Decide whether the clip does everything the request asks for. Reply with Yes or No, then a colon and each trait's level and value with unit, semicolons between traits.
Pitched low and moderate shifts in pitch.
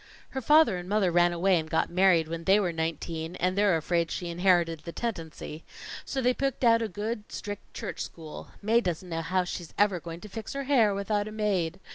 No: medium, 185 Hz; average, 4.0 semitones